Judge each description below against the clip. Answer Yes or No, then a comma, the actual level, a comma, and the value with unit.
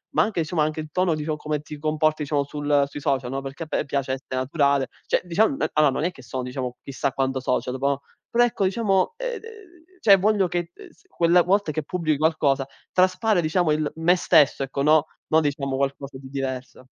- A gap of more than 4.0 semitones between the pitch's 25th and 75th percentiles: Yes, average, 4.4 semitones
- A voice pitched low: No, medium, 150 Hz